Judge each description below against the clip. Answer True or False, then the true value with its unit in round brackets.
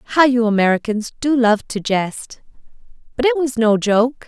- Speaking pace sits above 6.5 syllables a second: False (4.4 syllables/s)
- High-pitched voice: True (230 Hz)